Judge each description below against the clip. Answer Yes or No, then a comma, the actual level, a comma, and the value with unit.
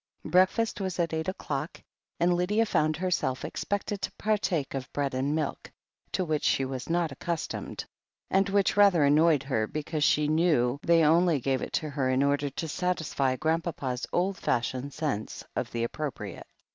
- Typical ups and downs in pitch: Yes, average, 4.5 semitones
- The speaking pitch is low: No, medium, 155 Hz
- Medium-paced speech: Yes, average, 170 wpm